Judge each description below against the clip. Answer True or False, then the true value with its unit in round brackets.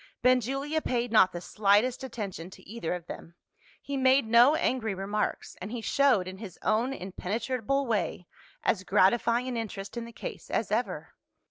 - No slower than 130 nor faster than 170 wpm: True (165 wpm)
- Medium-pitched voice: False (225 Hz)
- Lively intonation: False (4.5 semitones)